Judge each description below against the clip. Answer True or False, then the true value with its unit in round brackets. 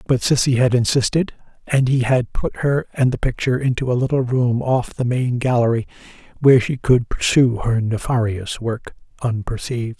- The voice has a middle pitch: False (125 Hz)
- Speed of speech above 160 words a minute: True (170 wpm)